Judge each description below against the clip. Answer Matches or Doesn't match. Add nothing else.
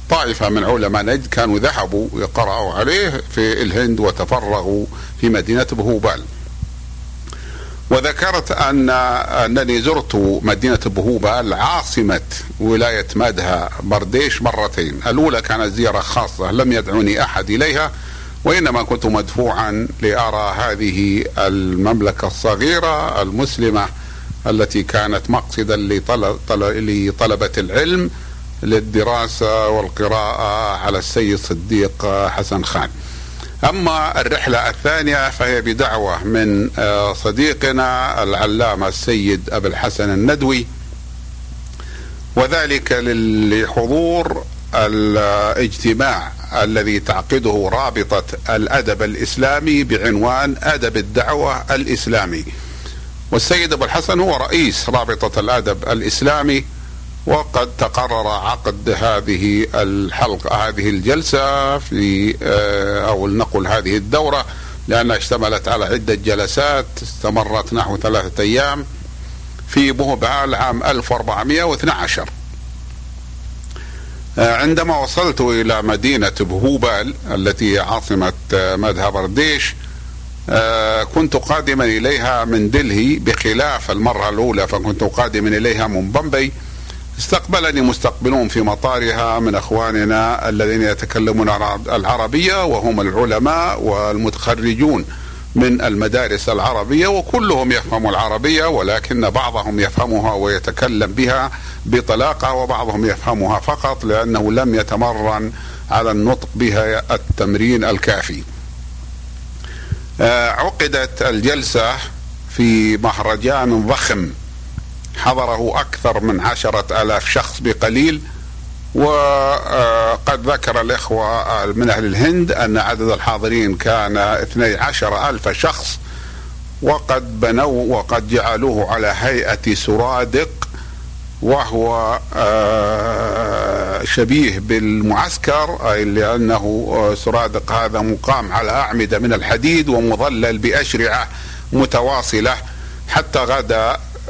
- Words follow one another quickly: Doesn't match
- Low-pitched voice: Matches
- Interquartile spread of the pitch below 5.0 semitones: Matches